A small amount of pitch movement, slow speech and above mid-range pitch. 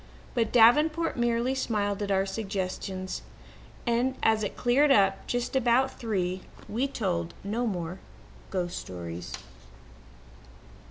No: average, 4.4 semitones; slow, 120 wpm; high, 215 Hz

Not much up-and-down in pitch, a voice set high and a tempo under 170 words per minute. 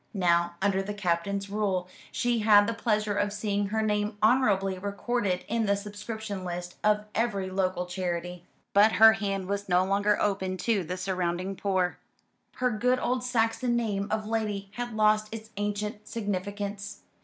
Yes: narrow, 2.3 semitones; high, 205 Hz; average, 160 wpm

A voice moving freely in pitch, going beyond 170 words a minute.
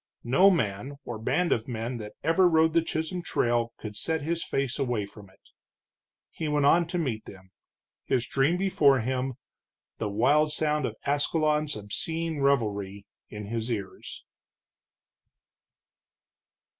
No: wide, 6.2 semitones; average, 140 wpm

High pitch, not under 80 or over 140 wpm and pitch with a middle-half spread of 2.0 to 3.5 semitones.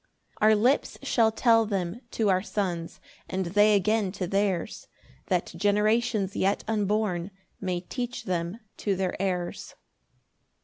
Yes: high, 200 Hz; slow, 135 wpm; average, 2.9 semitones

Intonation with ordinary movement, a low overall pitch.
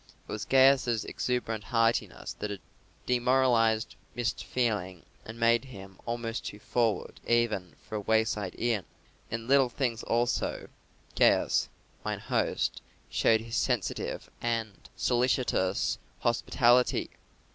No: narrow, 2.0 semitones; low, 115 Hz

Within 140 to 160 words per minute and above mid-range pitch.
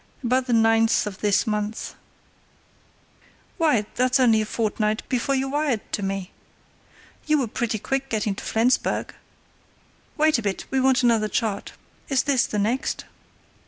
Yes: average, 150 wpm; high, 230 Hz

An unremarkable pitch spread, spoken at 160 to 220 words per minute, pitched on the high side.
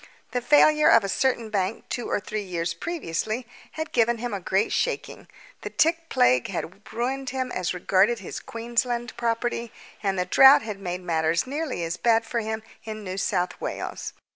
Yes: average, 4.7 semitones; average, 180 wpm; high, 225 Hz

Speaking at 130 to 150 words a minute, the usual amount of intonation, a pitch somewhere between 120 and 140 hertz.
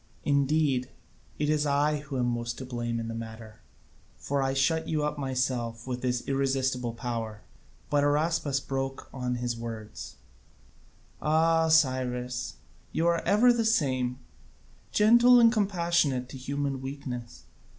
Yes: average, 140 wpm; average, 3.6 semitones; low, 135 Hz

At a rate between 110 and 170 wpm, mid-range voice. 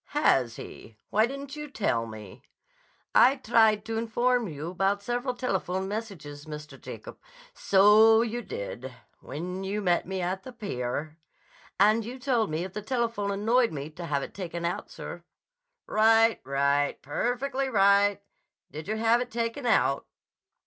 No: average, 155 wpm; high, 205 Hz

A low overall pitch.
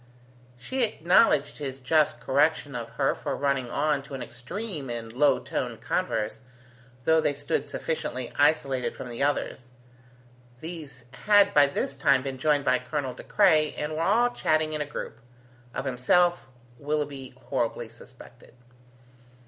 No: medium, 145 Hz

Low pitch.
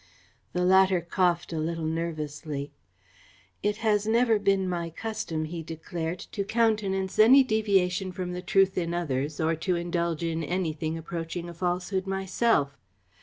No: medium, 180 Hz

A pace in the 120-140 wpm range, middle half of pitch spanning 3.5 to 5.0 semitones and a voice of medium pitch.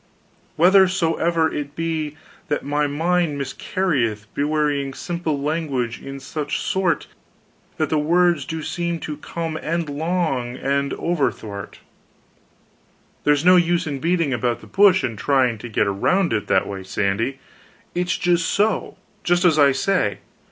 Yes: slow, 135 wpm; average, 4.1 semitones; medium, 155 Hz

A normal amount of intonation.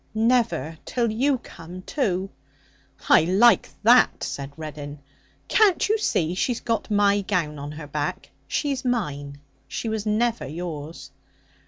No: wide, 7.6 semitones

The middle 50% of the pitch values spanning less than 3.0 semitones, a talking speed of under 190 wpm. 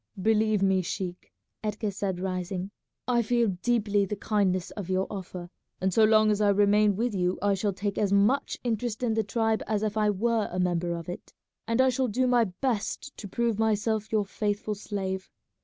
No: narrow, 2.6 semitones; average, 195 wpm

